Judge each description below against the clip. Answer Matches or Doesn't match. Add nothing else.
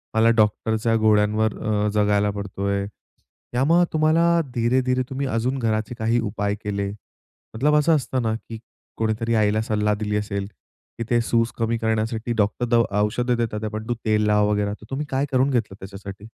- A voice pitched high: Doesn't match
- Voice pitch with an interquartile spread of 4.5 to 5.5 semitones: Doesn't match